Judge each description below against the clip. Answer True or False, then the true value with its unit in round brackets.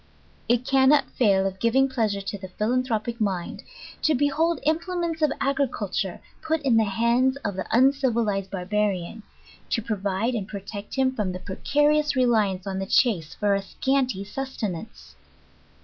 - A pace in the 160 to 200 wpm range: False (150 wpm)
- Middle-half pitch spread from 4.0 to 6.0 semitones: True (5.3 semitones)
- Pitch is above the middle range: True (225 Hz)